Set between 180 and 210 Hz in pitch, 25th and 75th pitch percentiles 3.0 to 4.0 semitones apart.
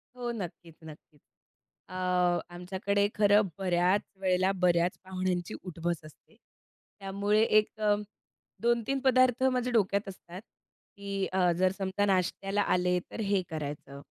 No: high, 190 Hz; narrow, 2.4 semitones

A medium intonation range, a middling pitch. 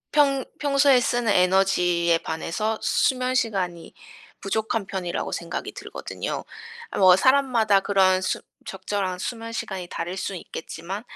No: average, 4.6 semitones; high, 195 Hz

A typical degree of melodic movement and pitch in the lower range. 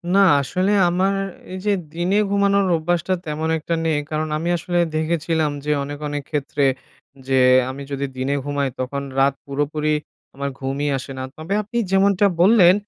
No: average, 4.4 semitones; medium, 155 Hz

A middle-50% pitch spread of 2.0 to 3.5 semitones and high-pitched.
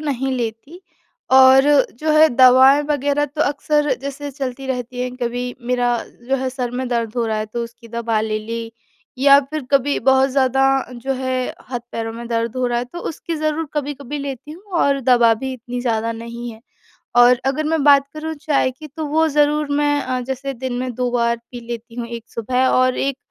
Yes: average, 3.0 semitones; very high, 255 Hz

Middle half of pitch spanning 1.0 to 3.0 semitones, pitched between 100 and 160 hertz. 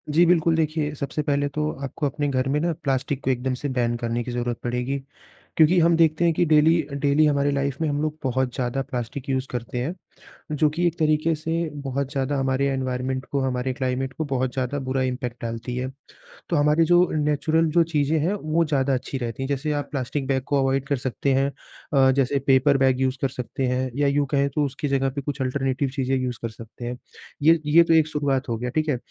Yes: average, 2.7 semitones; medium, 140 Hz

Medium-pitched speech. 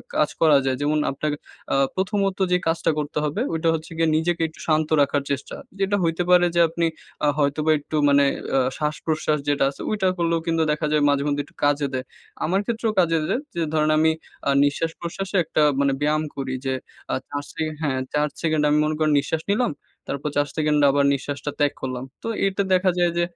Yes: medium, 155 Hz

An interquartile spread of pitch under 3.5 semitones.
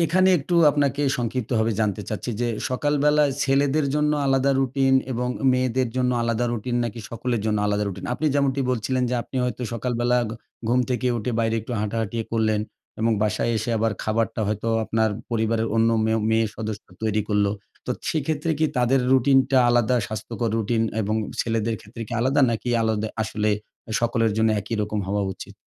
Yes: average, 3.0 semitones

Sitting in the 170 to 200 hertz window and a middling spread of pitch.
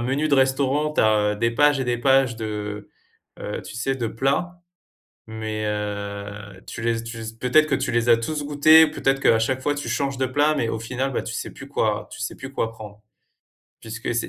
No: low, 120 Hz; average, 3.8 semitones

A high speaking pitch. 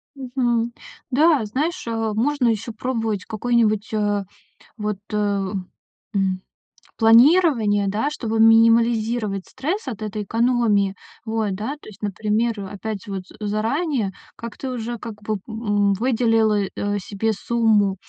Yes: high, 220 Hz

